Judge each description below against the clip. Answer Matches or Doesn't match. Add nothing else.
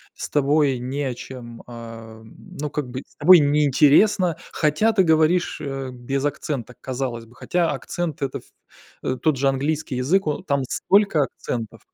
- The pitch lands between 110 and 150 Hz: Matches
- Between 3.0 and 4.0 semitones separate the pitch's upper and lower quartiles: Matches